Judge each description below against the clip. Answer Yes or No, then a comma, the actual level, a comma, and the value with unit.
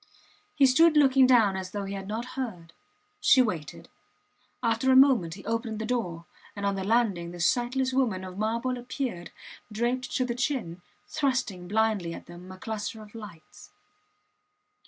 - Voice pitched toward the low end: No, high, 220 Hz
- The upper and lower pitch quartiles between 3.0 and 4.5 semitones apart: No, average, 5.1 semitones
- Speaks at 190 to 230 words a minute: No, average, 165 wpm